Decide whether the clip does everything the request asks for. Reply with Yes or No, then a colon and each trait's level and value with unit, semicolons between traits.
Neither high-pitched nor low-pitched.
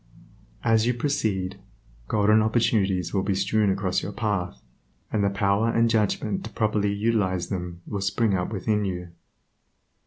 No: low, 100 Hz